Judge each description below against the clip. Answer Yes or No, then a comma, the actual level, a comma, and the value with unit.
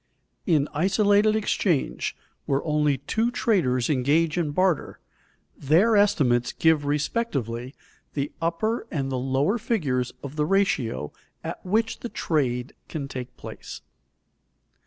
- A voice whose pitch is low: No, medium, 150 Hz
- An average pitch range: No, wide, 7.1 semitones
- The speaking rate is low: Yes, slow, 120 wpm